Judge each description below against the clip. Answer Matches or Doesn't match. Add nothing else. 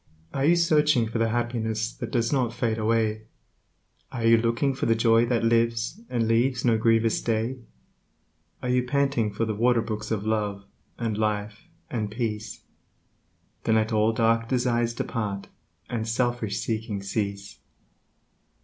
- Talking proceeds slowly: Doesn't match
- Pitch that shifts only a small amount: Matches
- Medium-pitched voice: Doesn't match